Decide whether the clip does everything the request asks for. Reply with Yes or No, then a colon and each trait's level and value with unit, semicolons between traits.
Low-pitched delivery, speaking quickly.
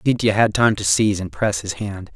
Yes: low, 100 Hz; fast, 250 wpm